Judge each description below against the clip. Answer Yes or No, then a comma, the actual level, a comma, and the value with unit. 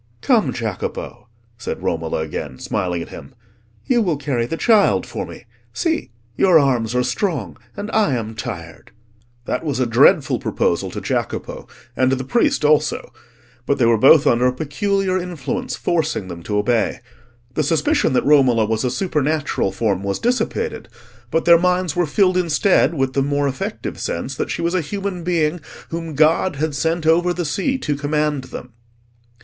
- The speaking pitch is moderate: Yes, medium, 150 Hz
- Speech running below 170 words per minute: No, average, 175 wpm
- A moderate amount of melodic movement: No, wide, 6.1 semitones